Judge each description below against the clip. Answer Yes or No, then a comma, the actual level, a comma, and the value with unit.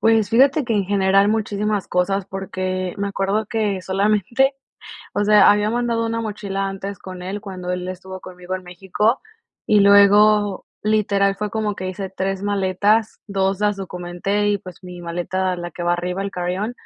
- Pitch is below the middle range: No, high, 195 Hz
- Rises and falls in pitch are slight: Yes, narrow, 2.1 semitones